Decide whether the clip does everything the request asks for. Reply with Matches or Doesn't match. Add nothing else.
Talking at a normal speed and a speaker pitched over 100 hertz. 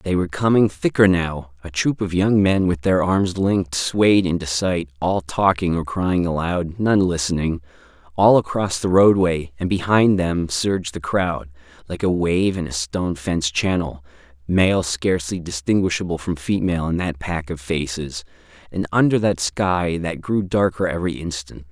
Doesn't match